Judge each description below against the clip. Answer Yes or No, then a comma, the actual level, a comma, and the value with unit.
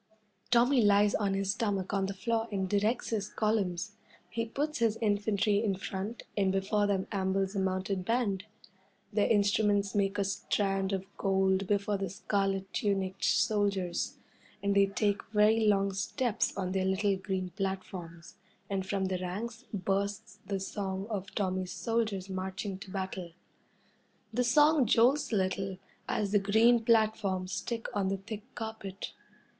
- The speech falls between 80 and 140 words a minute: No, average, 150 wpm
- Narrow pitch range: Yes, narrow, 2.0 semitones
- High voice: Yes, high, 200 Hz